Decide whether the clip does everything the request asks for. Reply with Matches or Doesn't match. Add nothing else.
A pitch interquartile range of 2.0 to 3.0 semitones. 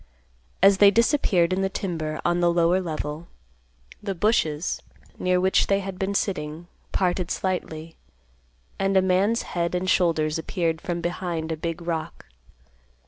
Matches